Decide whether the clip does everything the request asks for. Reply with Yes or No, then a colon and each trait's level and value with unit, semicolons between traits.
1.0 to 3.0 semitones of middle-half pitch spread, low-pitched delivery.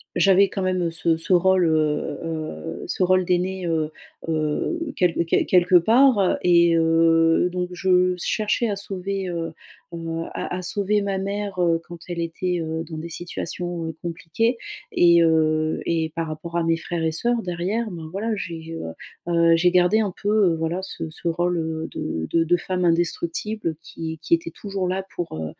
No: narrow, 2.4 semitones; medium, 175 Hz